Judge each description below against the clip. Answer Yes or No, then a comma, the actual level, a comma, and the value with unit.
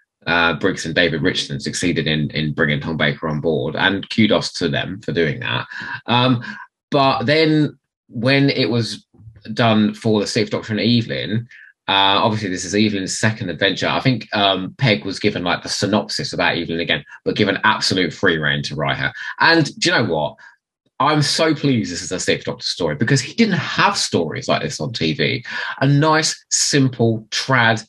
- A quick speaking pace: No, average, 185 wpm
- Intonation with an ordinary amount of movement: No, wide, 7.7 semitones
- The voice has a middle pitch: No, low, 110 Hz